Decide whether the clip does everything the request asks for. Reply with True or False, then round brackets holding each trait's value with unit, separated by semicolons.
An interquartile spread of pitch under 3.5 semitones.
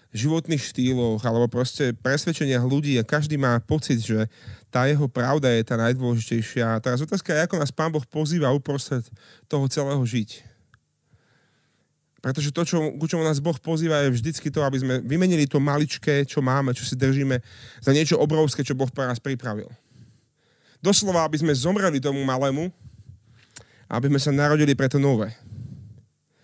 False (3.8 semitones)